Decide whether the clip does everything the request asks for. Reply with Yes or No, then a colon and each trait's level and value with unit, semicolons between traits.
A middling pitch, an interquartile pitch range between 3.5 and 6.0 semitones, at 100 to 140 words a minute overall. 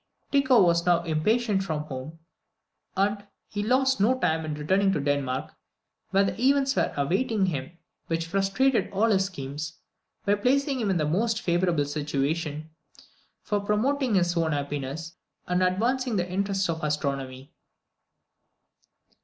Yes: medium, 180 Hz; wide, 5.4 semitones; slow, 135 wpm